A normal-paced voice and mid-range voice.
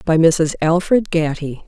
Yes: average, 145 wpm; medium, 165 Hz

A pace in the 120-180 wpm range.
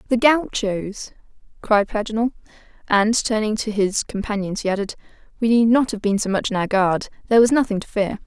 No: average, 190 wpm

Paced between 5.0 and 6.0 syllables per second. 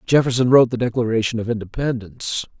No: 6.7 syllables/s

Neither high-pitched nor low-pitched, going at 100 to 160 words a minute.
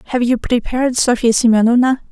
No: high, 240 Hz; average, 140 wpm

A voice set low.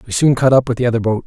Yes: low, 120 Hz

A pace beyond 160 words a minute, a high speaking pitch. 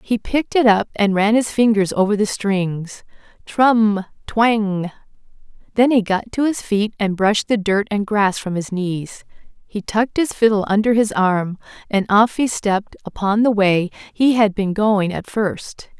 Yes: average, 175 wpm; high, 210 Hz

